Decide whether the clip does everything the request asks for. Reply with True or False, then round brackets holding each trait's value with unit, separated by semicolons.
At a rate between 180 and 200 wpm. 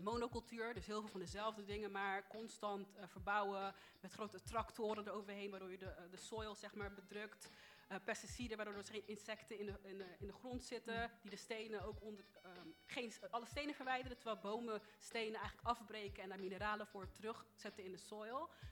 True (195 wpm)